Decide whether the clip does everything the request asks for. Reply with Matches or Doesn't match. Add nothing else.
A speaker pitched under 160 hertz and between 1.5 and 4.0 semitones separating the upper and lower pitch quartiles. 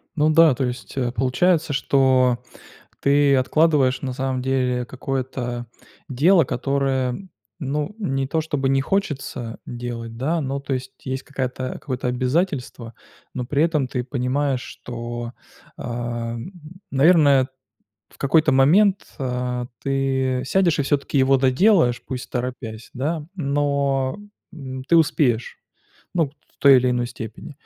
Matches